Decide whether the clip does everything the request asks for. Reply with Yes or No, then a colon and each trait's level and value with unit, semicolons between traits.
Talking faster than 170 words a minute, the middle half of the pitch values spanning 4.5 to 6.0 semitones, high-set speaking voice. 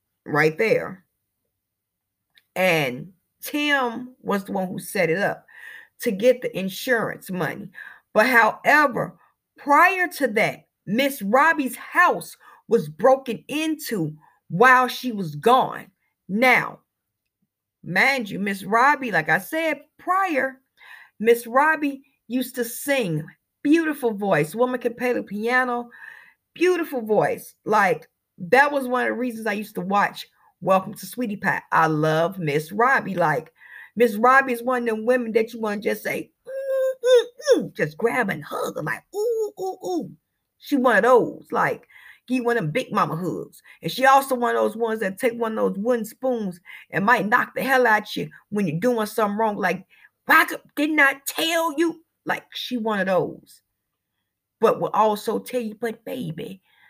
No: average, 165 wpm; average, 4.8 semitones; high, 245 Hz